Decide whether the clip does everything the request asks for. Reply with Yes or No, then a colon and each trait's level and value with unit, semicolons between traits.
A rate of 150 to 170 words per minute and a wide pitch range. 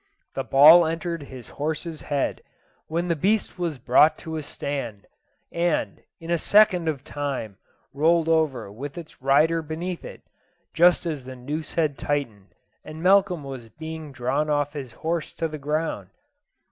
No: average, 160 wpm; average, 3.1 semitones